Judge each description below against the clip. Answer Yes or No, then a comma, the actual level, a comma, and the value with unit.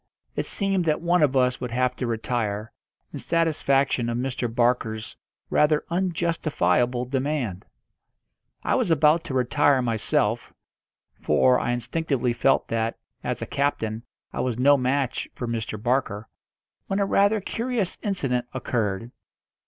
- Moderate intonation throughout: Yes, average, 4.5 semitones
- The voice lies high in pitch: No, low, 130 Hz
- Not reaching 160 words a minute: Yes, slow, 135 wpm